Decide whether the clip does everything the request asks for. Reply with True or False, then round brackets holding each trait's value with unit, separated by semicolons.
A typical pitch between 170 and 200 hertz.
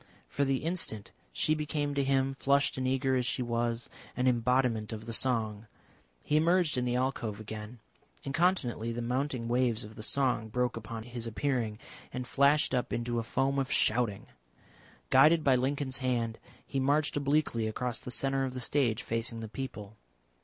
False (125 Hz)